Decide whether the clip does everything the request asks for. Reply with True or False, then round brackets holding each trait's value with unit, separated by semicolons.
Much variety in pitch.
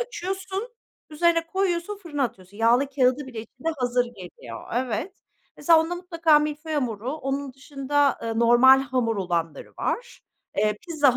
True (5.7 semitones)